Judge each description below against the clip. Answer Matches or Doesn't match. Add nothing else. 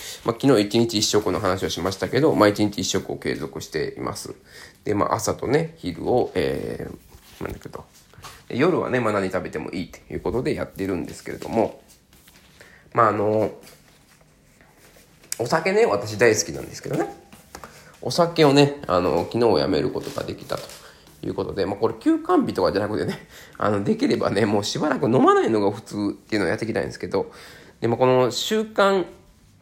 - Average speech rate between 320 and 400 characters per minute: Matches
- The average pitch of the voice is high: Doesn't match